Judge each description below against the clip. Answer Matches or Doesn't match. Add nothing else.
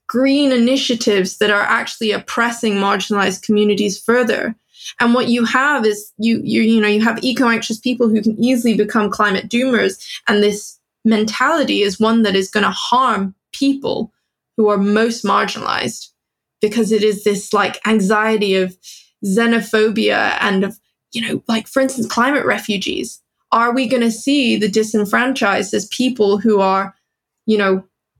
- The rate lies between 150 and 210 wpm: Matches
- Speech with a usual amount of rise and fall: Doesn't match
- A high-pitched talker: Matches